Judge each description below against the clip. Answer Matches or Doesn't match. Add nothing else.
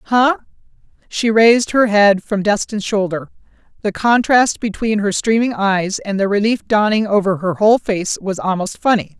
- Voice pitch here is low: Doesn't match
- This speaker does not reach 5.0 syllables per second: Matches